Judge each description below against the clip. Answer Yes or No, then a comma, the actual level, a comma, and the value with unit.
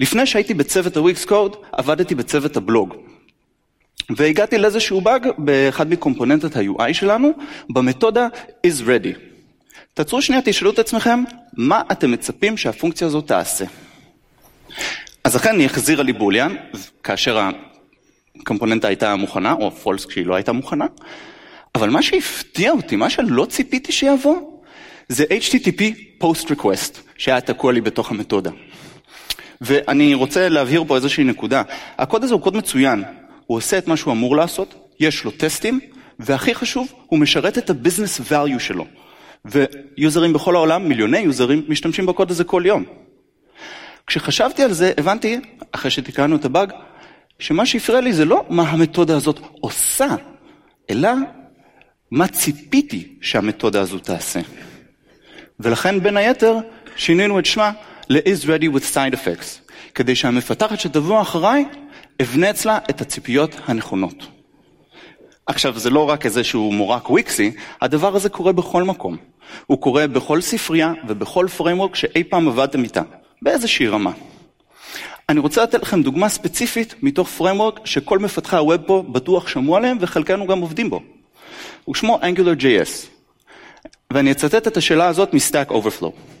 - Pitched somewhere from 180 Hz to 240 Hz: Yes, medium, 185 Hz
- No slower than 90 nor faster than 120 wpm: No, average, 135 wpm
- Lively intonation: Yes, wide, 7.6 semitones